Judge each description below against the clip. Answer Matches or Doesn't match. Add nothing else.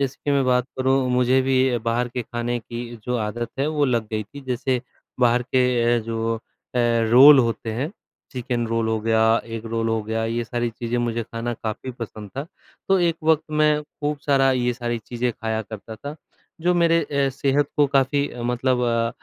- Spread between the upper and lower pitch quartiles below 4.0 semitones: Matches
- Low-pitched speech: Matches